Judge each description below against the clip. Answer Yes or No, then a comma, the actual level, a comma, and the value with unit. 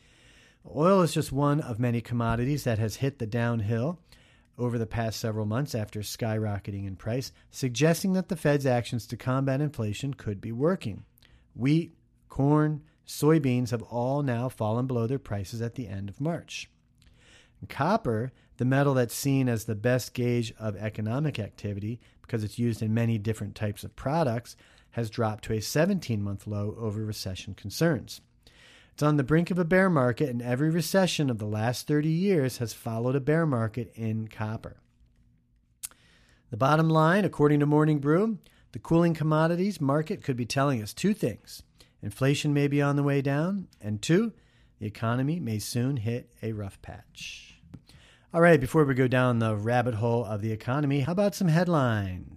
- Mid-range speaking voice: No, low, 125 Hz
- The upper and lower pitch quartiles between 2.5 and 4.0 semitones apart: No, average, 5.2 semitones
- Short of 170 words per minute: No, average, 175 wpm